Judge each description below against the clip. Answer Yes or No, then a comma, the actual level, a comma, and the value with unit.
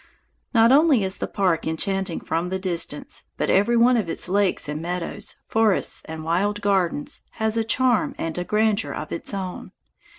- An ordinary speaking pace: Yes, average, 175 wpm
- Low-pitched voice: No, high, 195 Hz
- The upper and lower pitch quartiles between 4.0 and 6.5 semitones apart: Yes, average, 4.5 semitones